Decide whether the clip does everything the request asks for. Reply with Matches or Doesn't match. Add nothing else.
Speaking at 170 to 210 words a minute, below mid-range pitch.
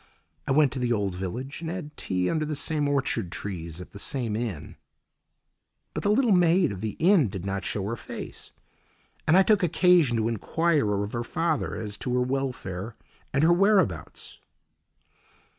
Matches